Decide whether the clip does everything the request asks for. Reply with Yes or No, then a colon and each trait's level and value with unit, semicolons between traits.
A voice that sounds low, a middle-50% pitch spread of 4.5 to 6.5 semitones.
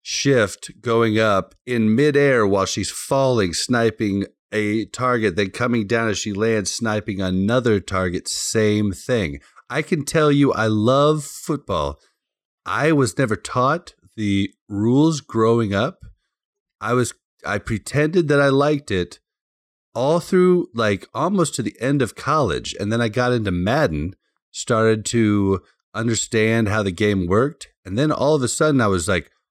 Yes: low, 110 Hz; average, 5.2 semitones